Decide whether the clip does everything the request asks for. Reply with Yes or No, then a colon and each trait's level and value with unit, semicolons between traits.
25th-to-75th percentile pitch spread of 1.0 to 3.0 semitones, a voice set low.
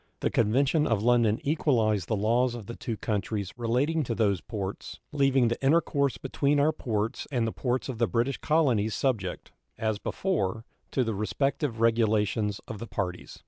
No: average, 4.1 semitones; low, 115 Hz